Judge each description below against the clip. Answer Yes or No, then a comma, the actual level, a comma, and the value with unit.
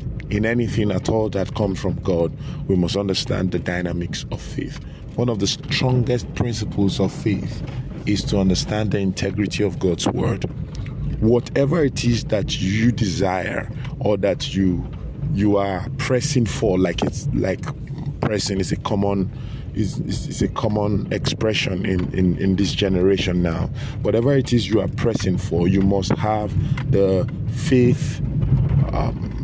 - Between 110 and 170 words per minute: Yes, average, 155 wpm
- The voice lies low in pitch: Yes, low, 110 Hz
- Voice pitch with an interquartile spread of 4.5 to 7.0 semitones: Yes, average, 5.1 semitones